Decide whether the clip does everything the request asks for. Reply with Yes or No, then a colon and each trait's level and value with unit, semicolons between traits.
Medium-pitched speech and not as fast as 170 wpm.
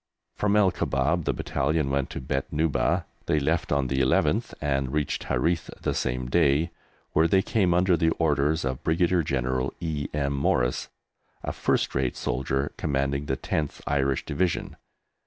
No: very low, 70 Hz; average, 160 wpm